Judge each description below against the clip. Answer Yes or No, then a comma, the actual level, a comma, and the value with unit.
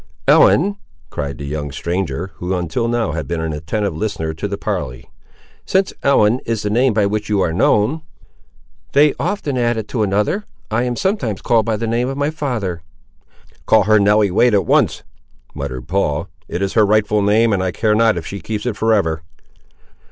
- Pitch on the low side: Yes, low, 105 Hz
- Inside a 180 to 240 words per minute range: Yes, average, 195 wpm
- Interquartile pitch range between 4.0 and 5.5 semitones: Yes, average, 4.6 semitones